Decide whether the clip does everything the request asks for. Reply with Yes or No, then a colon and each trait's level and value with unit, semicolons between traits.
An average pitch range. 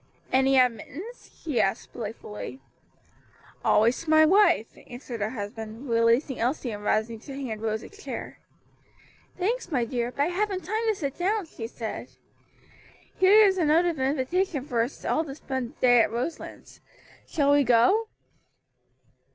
No: wide, 6.9 semitones